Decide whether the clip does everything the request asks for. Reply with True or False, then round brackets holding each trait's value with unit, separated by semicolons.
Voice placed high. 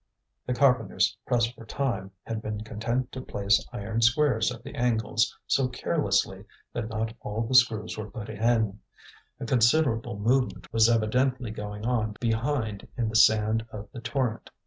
False (115 Hz)